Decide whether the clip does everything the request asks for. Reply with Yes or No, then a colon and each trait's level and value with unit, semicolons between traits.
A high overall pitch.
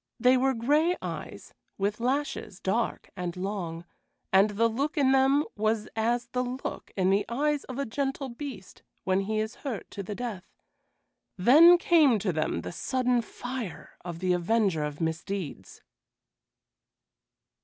Yes: high, 225 Hz